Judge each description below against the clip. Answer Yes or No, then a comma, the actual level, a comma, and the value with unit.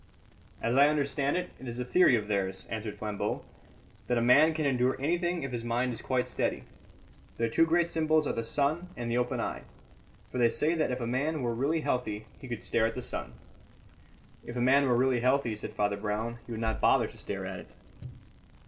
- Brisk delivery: Yes, fast, 220 wpm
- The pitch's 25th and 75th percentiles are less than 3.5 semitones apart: No, average, 3.8 semitones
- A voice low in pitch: Yes, low, 125 Hz